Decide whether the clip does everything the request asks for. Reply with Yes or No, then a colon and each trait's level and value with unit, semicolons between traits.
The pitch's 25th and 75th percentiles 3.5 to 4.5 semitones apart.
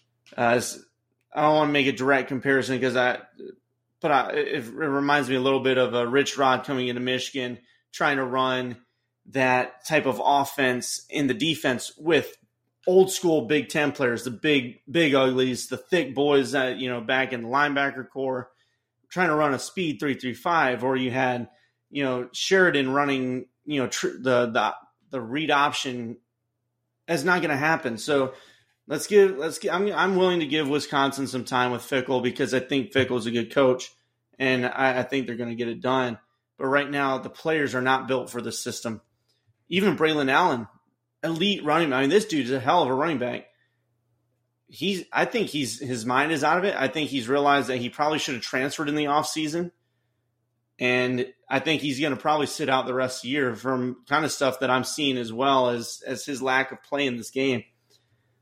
No: narrow, 2.5 semitones